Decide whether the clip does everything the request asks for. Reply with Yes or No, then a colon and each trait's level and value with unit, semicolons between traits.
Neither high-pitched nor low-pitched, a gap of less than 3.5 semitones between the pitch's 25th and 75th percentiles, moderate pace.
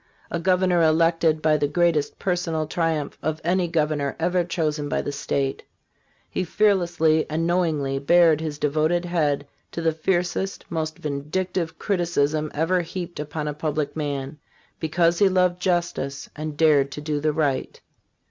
Yes: medium, 160 Hz; narrow, 2.6 semitones; average, 155 wpm